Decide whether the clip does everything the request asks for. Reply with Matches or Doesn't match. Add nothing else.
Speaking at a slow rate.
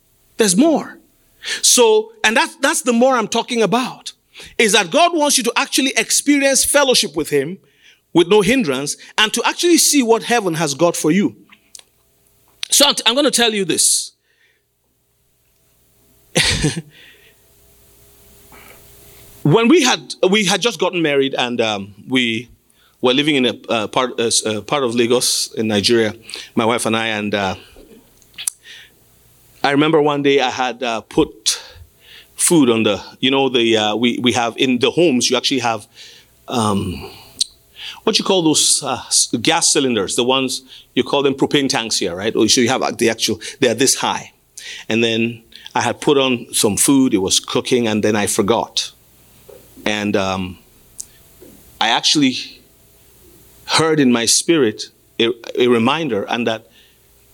Doesn't match